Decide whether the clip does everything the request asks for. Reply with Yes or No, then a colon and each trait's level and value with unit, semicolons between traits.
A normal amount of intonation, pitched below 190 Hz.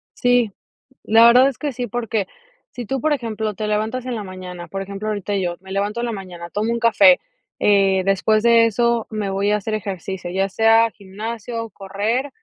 No: average, 3.2 semitones; high, 215 Hz